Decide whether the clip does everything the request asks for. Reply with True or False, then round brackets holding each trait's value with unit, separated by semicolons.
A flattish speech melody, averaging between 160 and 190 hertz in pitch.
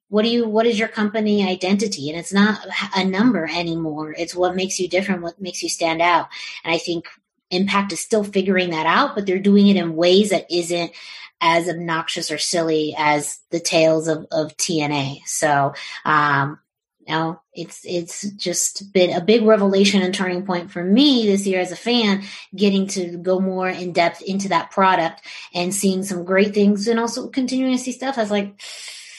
False (3.2 semitones; 185 Hz)